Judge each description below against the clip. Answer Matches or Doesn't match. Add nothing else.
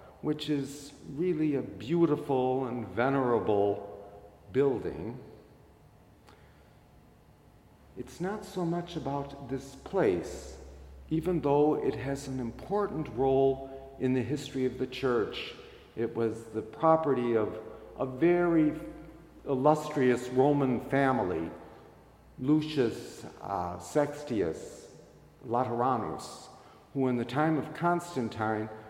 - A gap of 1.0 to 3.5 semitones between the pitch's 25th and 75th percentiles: Doesn't match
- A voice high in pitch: Doesn't match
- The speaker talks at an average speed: Doesn't match